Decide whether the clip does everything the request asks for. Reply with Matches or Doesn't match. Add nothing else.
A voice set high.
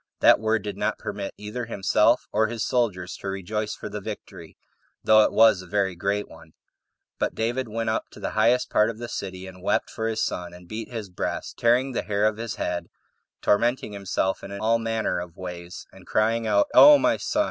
Doesn't match